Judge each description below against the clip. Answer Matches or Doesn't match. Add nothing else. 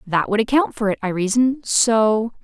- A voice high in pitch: Matches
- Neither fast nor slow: Matches